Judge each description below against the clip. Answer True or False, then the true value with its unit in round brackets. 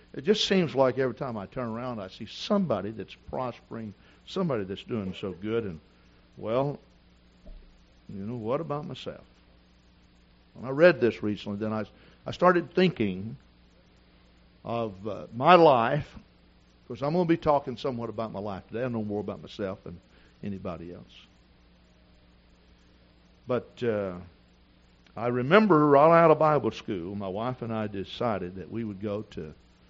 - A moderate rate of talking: True (155 wpm)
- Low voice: True (100 Hz)